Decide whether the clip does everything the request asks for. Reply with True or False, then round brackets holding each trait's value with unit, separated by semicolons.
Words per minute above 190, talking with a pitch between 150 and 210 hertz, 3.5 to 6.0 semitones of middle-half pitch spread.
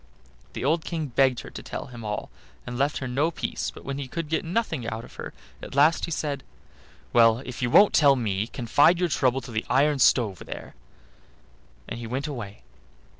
False (200 wpm; 130 Hz; 4.2 semitones)